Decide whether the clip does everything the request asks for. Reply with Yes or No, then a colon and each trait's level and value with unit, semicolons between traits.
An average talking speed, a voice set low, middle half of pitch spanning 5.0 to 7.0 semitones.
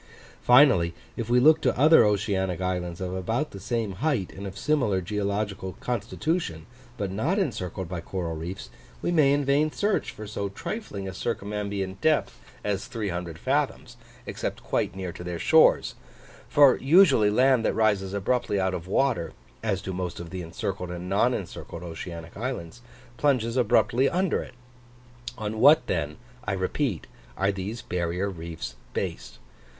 Yes: average, 155 wpm; low, 100 Hz; average, 5.3 semitones